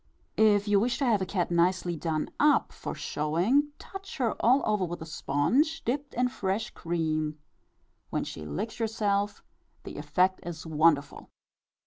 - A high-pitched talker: Yes, high, 200 Hz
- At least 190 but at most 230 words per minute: No, average, 160 wpm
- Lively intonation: Yes, wide, 6.1 semitones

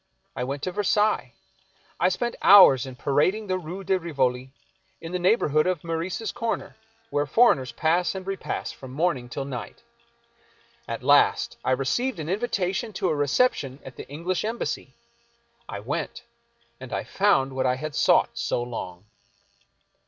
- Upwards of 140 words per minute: Yes, average, 160 wpm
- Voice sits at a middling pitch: Yes, medium, 165 Hz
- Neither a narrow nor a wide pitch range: No, wide, 6.3 semitones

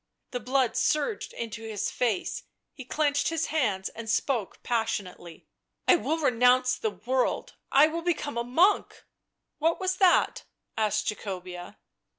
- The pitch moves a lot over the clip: Yes, wide, 6.0 semitones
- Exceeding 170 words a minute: No, average, 160 wpm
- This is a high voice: Yes, very high, 250 Hz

